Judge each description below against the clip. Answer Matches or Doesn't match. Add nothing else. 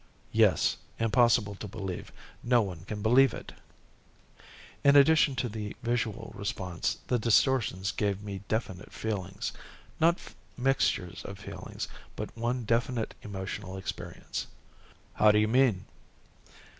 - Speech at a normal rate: Doesn't match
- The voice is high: Doesn't match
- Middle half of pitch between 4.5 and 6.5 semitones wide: Doesn't match